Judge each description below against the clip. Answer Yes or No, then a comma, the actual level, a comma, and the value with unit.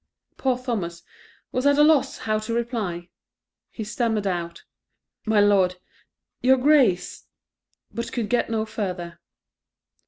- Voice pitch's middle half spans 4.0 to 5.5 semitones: Yes, average, 5.0 semitones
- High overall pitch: Yes, high, 220 Hz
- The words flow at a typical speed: No, slow, 125 wpm